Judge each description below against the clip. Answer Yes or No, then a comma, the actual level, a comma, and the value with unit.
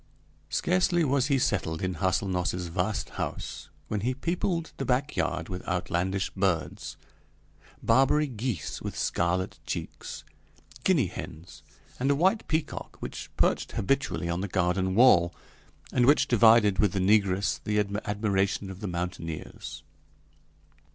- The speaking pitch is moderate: No, low, 100 Hz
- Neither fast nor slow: No, slow, 130 wpm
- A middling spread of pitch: No, wide, 6.0 semitones